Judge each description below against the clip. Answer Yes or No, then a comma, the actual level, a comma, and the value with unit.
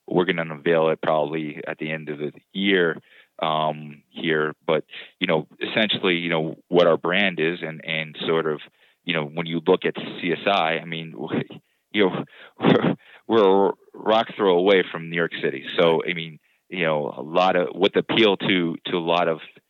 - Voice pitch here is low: Yes, very low, 80 Hz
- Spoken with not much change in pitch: Yes, narrow, 1.6 semitones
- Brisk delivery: No, average, 195 wpm